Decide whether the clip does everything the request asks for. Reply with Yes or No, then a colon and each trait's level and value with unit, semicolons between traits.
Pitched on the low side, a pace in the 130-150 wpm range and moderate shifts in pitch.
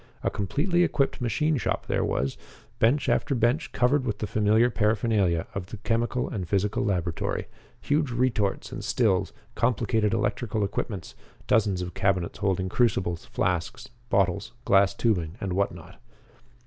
Yes: low, 105 Hz; average, 145 wpm; average, 4.3 semitones